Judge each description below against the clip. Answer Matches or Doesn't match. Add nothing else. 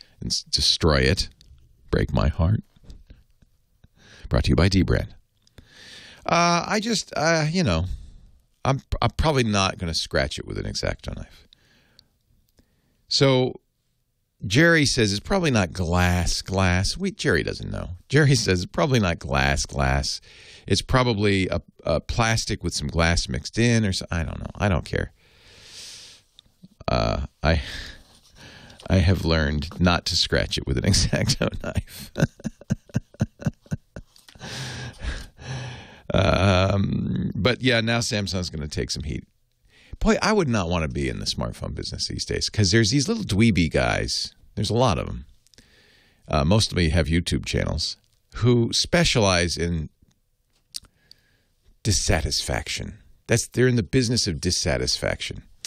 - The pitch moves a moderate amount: Doesn't match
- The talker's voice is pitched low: Matches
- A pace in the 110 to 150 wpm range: Matches